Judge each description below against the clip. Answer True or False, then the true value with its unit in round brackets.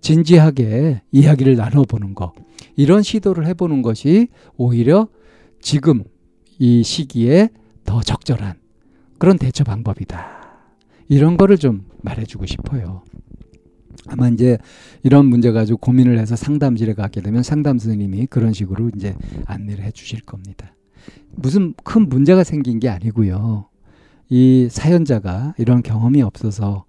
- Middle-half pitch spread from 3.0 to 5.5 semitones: True (5.2 semitones)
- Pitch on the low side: True (120 Hz)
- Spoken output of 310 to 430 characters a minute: False (285 characters per minute)